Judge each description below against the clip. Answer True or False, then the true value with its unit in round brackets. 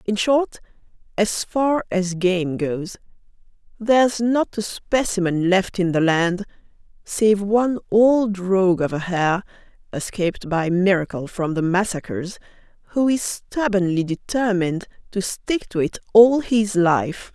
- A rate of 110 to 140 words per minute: True (135 wpm)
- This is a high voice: True (195 Hz)